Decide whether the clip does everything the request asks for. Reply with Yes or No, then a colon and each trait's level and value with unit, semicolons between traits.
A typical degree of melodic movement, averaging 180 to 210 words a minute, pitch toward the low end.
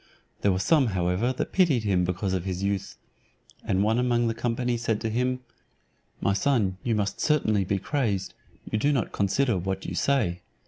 Yes: average, 4.5 semitones; average, 185 wpm; low, 110 Hz